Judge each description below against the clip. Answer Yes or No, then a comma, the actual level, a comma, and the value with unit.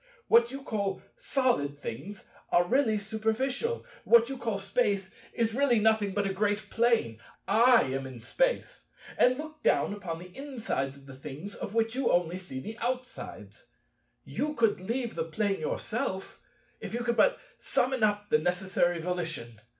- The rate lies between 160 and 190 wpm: Yes, average, 165 wpm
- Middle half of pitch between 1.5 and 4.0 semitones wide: No, average, 5.3 semitones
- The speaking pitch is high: Yes, high, 210 Hz